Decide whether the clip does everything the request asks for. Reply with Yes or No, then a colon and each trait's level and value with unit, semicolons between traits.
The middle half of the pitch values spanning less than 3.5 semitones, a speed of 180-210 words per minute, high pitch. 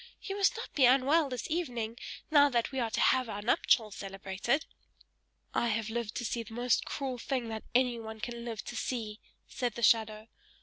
Yes: average, 2.7 semitones; average, 190 wpm; high, 235 Hz